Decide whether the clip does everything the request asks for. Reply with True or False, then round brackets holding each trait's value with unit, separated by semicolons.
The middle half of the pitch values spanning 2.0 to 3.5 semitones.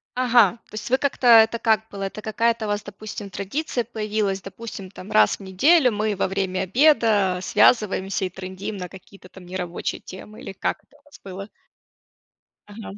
True (3.2 semitones)